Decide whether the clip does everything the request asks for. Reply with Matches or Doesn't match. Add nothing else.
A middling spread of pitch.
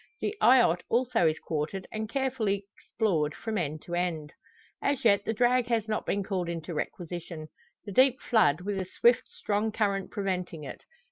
Matches